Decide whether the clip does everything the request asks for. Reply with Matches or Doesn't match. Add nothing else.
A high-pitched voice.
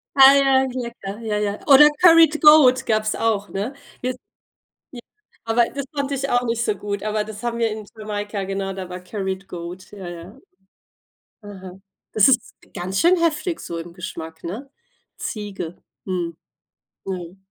Matches